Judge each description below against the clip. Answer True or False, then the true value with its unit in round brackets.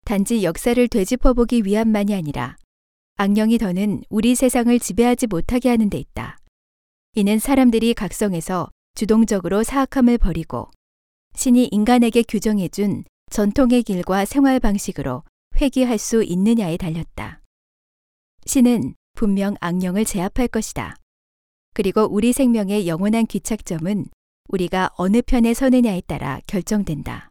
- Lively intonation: False (4.9 semitones)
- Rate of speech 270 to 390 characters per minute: True (305 characters per minute)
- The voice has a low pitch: False (210 Hz)